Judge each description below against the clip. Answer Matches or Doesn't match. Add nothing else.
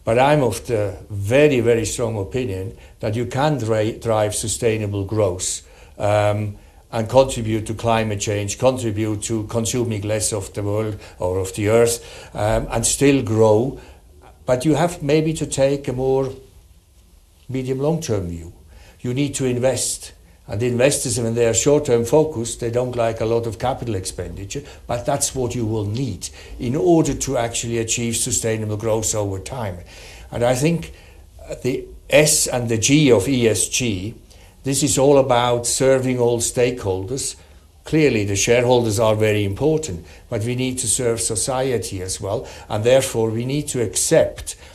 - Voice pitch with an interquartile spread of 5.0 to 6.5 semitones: Doesn't match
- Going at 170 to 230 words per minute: Doesn't match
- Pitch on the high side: Doesn't match